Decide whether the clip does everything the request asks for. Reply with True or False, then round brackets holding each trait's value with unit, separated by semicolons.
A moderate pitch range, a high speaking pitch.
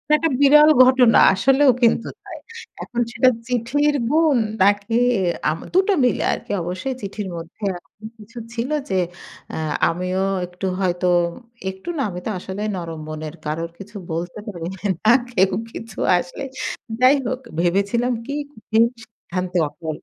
False (6.0 semitones; 205 Hz)